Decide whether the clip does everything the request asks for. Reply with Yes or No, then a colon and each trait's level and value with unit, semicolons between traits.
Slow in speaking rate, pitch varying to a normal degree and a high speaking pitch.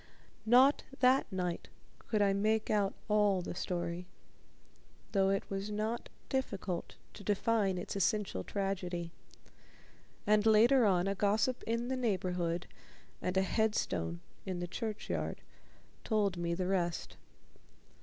Yes: slow, 125 wpm; average, 3.3 semitones; high, 195 Hz